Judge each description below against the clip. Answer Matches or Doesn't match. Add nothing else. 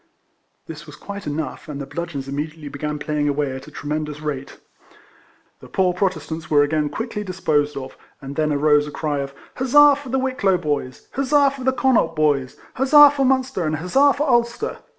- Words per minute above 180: Matches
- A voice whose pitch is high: Doesn't match